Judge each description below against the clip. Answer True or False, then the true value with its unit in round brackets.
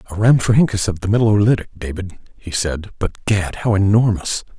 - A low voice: True (100 Hz)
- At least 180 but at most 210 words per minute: False (170 wpm)